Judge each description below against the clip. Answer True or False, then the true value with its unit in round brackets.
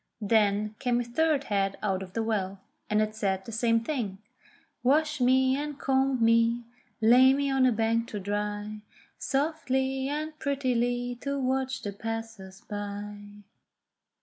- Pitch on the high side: True (230 Hz)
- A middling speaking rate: True (150 wpm)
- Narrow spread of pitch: False (4.2 semitones)